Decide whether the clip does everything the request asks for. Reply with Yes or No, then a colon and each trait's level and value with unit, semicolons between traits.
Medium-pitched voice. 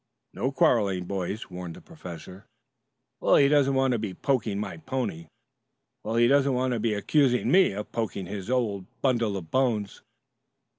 No: low, 115 Hz